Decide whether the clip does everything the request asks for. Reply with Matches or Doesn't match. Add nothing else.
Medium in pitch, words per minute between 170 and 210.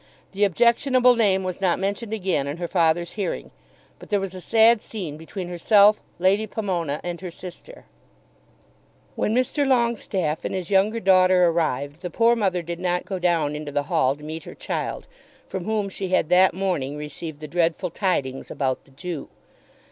Matches